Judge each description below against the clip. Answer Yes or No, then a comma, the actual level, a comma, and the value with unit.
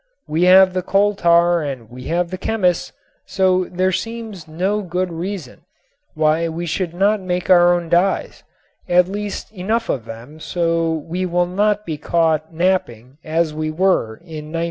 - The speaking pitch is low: No, medium, 175 Hz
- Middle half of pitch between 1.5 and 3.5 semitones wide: Yes, average, 2.8 semitones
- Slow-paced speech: No, average, 165 wpm